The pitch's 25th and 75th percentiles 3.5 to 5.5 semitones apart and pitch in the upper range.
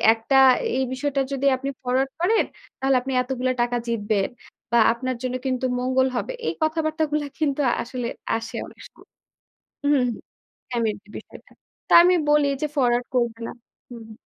No: average, 3.0 semitones; very high, 255 Hz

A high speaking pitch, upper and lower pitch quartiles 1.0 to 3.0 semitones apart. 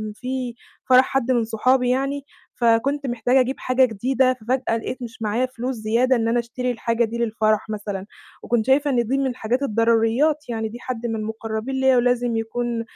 Yes: high, 240 Hz; narrow, 2.4 semitones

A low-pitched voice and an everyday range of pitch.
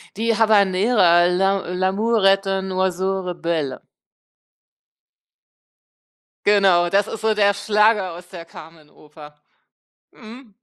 No: high, 190 Hz; average, 3.1 semitones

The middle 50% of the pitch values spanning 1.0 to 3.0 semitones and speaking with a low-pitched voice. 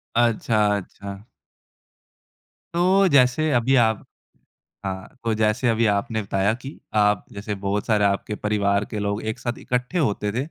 No: average, 3.4 semitones; low, 110 Hz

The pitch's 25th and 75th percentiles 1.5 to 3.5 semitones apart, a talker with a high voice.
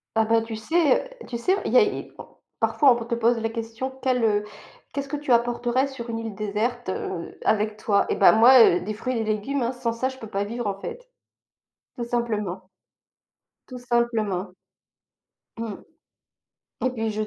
Yes: average, 2.8 semitones; high, 230 Hz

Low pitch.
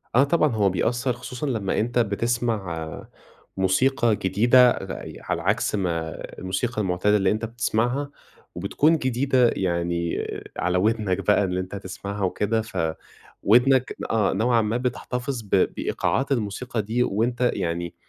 Yes: low, 110 Hz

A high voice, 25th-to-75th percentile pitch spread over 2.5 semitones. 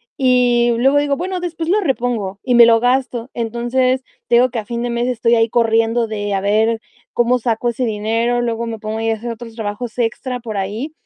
No: high, 235 Hz; narrow, 1.9 semitones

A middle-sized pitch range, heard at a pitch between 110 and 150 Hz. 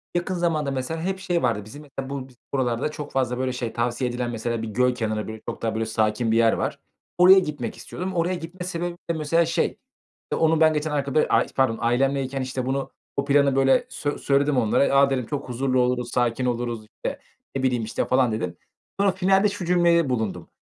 Yes: average, 4.8 semitones; low, 135 Hz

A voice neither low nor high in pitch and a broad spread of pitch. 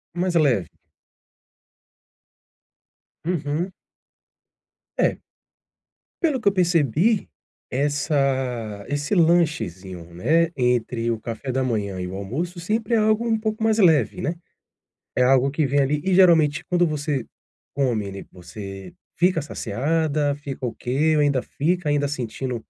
Yes: medium, 145 Hz; wide, 5.9 semitones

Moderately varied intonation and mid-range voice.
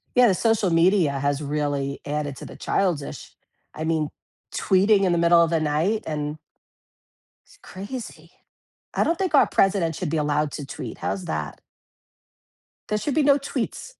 No: wide, 5.8 semitones; medium, 170 Hz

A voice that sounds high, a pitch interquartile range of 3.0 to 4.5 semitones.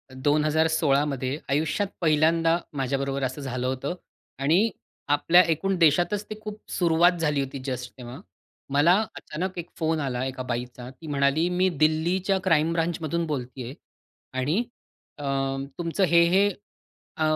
No: medium, 155 Hz; average, 3.8 semitones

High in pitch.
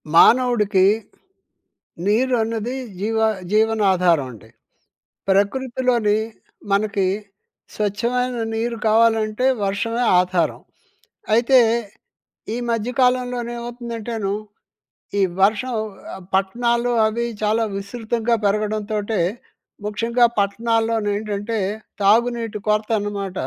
Yes: high, 220 Hz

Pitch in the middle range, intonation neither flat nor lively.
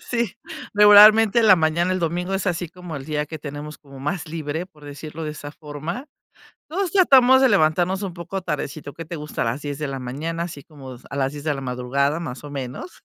Yes: medium, 155 Hz; average, 4.3 semitones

